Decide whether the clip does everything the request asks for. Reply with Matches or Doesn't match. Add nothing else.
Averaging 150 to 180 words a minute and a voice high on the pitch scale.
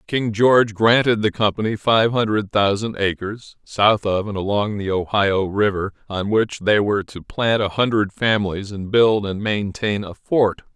Doesn't match